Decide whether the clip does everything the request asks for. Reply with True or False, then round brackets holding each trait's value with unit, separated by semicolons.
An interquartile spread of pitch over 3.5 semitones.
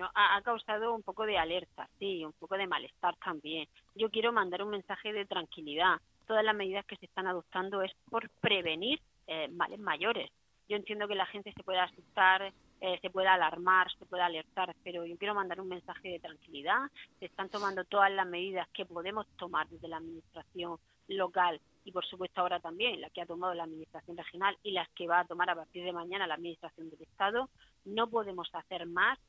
False (2.5 semitones)